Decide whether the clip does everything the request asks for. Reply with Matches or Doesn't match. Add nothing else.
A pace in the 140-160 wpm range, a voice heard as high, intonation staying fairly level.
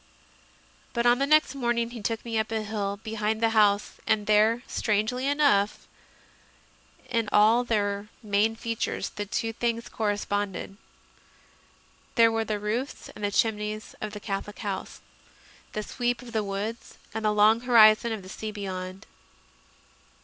Matches